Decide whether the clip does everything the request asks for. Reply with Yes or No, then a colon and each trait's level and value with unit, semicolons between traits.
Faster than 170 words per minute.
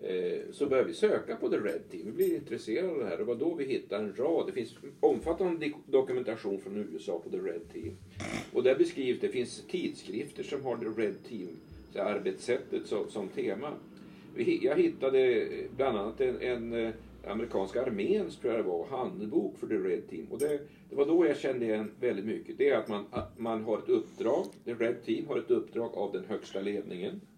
Yes: average, 190 wpm